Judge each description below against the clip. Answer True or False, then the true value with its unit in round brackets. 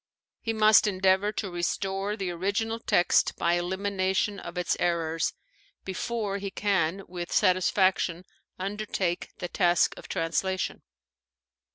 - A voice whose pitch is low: False (190 Hz)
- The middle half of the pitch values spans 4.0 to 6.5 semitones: False (2.4 semitones)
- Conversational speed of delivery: False (120 wpm)